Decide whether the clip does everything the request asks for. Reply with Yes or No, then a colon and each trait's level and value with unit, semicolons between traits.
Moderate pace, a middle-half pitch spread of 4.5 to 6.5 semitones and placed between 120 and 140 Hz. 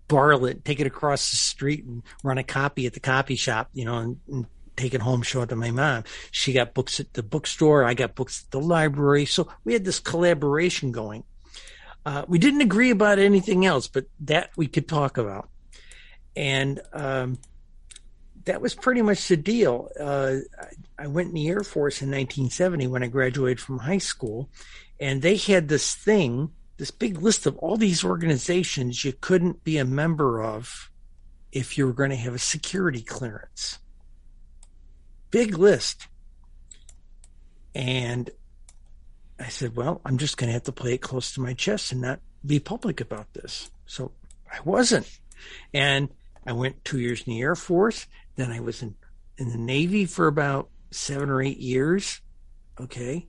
Yes: average, 180 wpm; average, 4.8 semitones; low, 135 Hz